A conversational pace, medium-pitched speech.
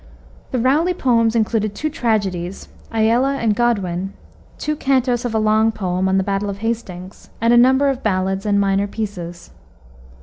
No: average, 165 wpm; high, 220 Hz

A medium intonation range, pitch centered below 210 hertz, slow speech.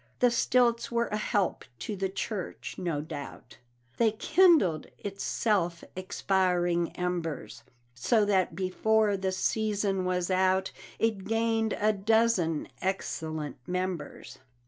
Yes: average, 3.6 semitones; high, 190 Hz; slow, 120 wpm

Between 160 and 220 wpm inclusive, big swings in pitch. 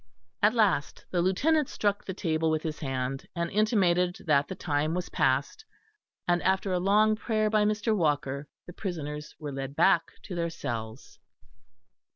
Yes: average, 165 wpm; wide, 5.7 semitones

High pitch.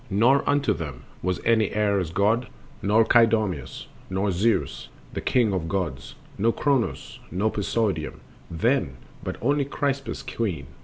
No: low, 105 Hz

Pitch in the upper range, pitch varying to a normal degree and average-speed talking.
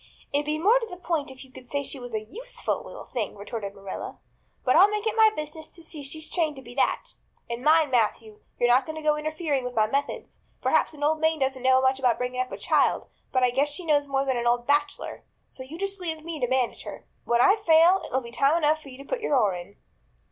No: very high, 280 Hz; average, 4.2 semitones; fast, 250 wpm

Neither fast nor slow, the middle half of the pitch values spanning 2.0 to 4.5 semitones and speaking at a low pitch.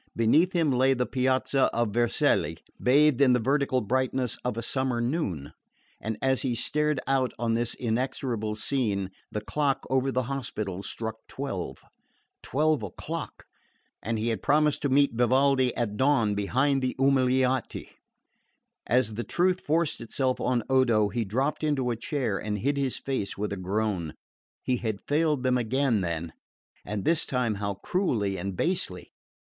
Yes: average, 160 wpm; average, 4.0 semitones; low, 125 Hz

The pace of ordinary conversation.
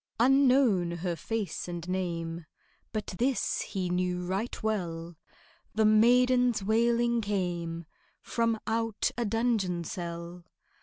No: slow, 110 wpm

